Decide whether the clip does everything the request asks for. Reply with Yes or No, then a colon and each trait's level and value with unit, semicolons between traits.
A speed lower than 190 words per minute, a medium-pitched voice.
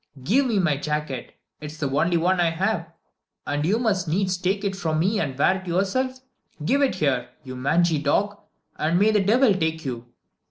No: average, 200 wpm; medium, 175 Hz